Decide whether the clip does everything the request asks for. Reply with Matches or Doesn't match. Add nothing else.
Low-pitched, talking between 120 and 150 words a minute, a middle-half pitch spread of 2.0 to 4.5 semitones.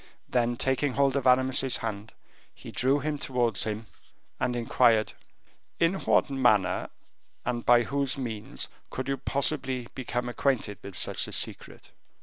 Matches